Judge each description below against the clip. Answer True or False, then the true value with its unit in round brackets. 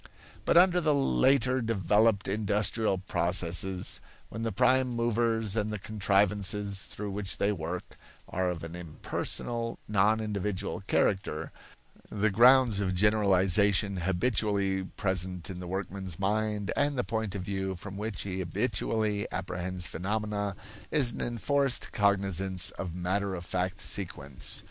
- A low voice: True (100 Hz)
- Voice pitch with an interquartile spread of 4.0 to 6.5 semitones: False (2.8 semitones)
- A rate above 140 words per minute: False (135 wpm)